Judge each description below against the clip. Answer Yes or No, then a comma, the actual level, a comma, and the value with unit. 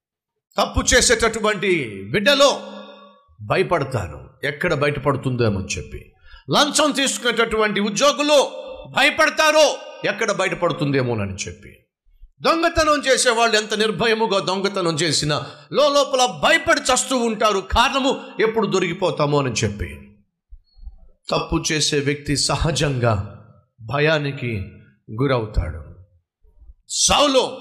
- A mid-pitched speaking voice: Yes, medium, 175 Hz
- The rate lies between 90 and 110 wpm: No, average, 80 wpm